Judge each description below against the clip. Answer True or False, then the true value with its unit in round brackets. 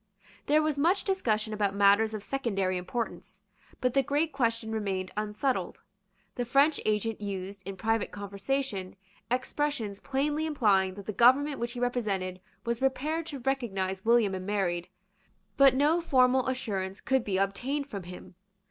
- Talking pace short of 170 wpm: True (150 wpm)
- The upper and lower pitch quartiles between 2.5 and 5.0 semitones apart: False (5.5 semitones)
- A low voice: False (230 Hz)